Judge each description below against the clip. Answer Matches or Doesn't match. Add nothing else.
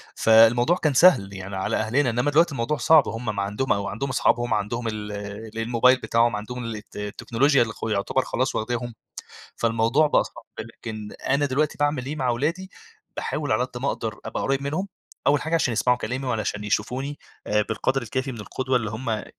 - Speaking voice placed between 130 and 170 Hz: Doesn't match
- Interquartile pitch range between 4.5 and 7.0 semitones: Doesn't match